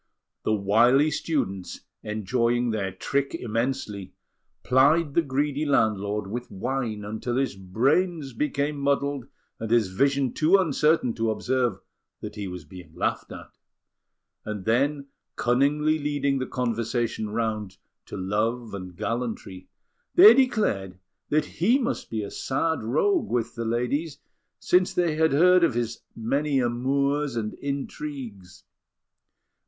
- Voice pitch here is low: Yes, low, 125 Hz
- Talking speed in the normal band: No, slow, 130 wpm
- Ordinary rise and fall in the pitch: Yes, average, 5.0 semitones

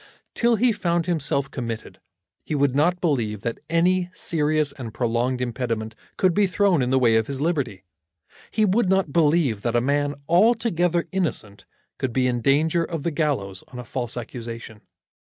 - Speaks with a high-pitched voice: No, medium, 145 Hz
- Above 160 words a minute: Yes, average, 175 wpm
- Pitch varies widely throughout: Yes, wide, 6.3 semitones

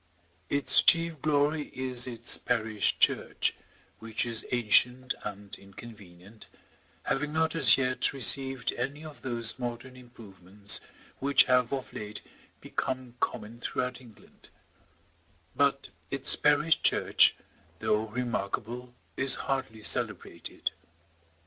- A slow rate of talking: Yes, slow, 110 wpm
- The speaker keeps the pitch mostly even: No, average, 3.3 semitones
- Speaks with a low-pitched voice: Yes, low, 125 Hz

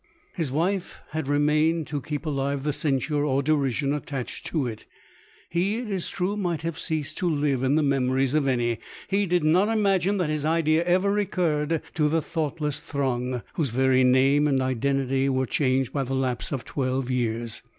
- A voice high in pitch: No, medium, 145 Hz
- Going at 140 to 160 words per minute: No, average, 180 wpm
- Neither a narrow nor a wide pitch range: Yes, average, 3.7 semitones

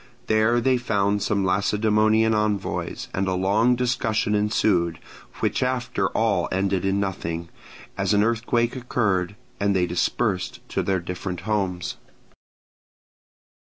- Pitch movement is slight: No, average, 3.0 semitones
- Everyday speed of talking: No, slow, 125 wpm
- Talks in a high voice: No, low, 105 Hz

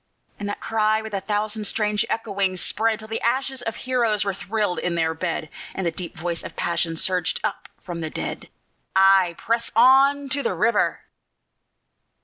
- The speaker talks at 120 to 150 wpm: No, average, 175 wpm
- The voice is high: Yes, high, 210 Hz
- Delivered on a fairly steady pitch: No, average, 4.0 semitones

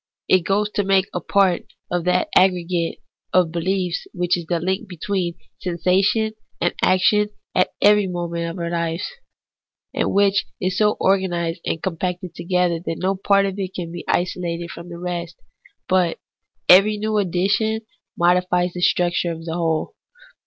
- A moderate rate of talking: Yes, average, 160 wpm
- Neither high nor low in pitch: Yes, medium, 180 Hz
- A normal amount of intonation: No, narrow, 2.1 semitones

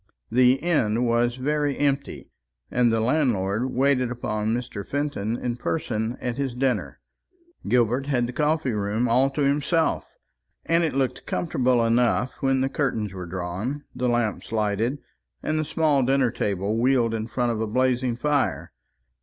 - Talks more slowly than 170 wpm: Yes, average, 155 wpm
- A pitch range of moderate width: Yes, average, 3.4 semitones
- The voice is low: Yes, low, 125 Hz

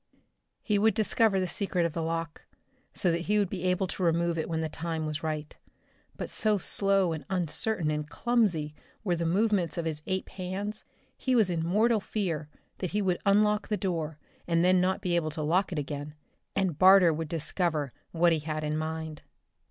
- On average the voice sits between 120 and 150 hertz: No, medium, 175 Hz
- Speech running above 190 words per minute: Yes, average, 200 wpm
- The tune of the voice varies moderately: Yes, average, 3.6 semitones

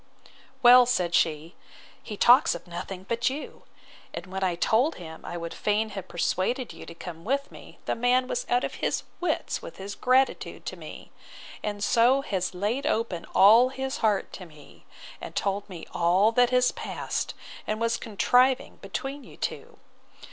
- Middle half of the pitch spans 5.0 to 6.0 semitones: Yes, wide, 5.5 semitones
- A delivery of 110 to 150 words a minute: No, average, 175 wpm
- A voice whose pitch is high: Yes, high, 215 Hz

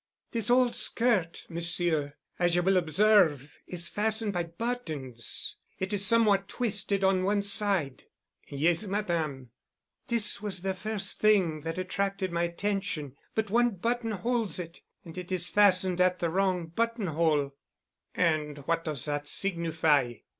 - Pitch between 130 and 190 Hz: Yes, medium, 185 Hz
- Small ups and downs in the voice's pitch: No, average, 4.1 semitones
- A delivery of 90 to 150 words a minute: Yes, average, 145 wpm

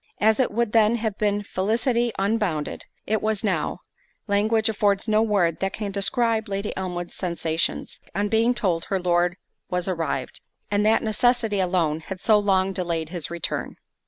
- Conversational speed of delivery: Yes, average, 160 wpm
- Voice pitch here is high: Yes, high, 200 Hz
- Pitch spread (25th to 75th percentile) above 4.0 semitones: No, average, 3.4 semitones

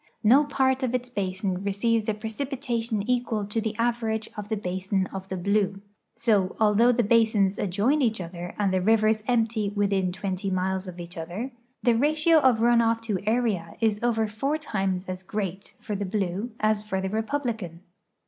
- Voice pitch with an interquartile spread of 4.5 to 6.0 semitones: No, average, 3.4 semitones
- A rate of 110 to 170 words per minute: No, average, 180 wpm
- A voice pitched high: Yes, high, 215 Hz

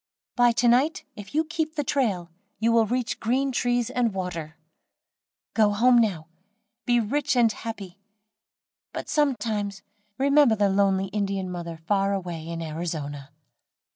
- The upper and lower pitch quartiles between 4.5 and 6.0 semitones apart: Yes, average, 5.2 semitones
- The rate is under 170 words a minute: Yes, average, 145 wpm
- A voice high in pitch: Yes, high, 210 Hz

